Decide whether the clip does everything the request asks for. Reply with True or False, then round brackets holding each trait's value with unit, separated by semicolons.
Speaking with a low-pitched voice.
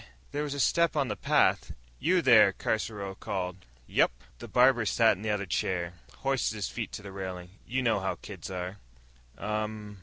True (105 Hz)